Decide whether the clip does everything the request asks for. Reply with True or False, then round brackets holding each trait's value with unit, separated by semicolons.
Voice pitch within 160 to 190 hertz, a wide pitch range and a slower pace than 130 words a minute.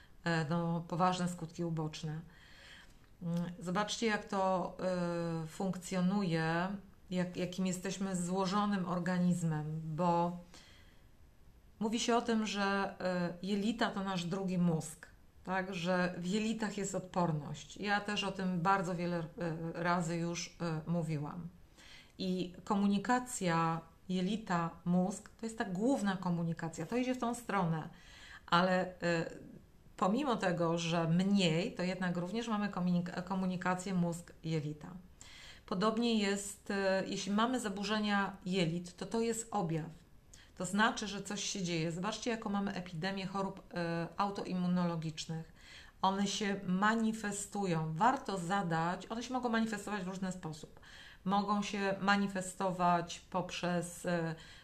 False (185 Hz; 2.8 semitones; 110 wpm)